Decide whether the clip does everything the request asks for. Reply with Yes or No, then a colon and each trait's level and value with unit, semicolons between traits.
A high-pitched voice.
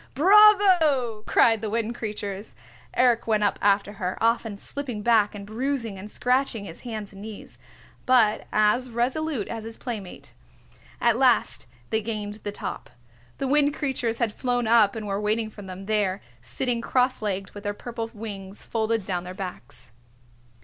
Yes: high, 220 Hz